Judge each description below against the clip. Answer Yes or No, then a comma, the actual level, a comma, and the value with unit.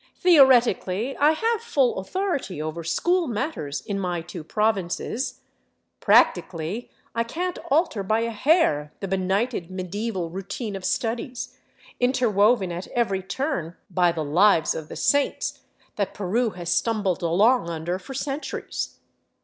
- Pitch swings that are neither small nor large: No, wide, 6.2 semitones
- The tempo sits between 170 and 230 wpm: No, slow, 135 wpm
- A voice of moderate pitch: No, high, 205 Hz